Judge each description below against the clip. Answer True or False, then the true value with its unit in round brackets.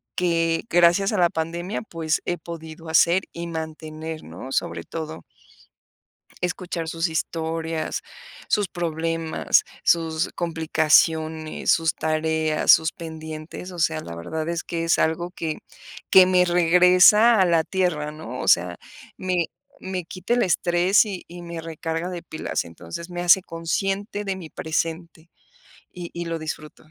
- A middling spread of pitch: False (1.9 semitones)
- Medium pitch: True (165 Hz)